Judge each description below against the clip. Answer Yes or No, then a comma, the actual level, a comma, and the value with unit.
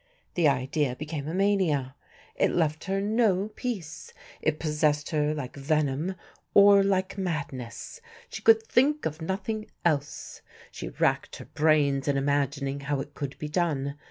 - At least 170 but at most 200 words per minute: No, average, 150 wpm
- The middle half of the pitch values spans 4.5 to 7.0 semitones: Yes, average, 5.2 semitones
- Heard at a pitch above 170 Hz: No, medium, 155 Hz